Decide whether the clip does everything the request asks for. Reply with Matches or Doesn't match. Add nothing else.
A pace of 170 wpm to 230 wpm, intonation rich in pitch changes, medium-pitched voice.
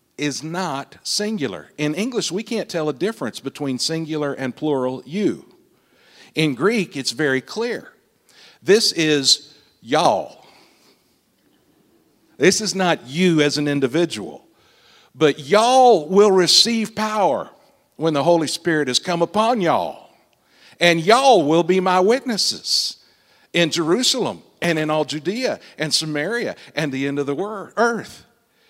Doesn't match